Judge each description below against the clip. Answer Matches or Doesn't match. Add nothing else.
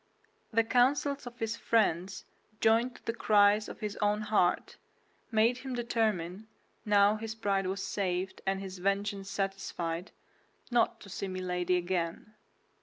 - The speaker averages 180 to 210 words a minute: Doesn't match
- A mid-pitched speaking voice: Doesn't match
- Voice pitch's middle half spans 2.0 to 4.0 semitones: Matches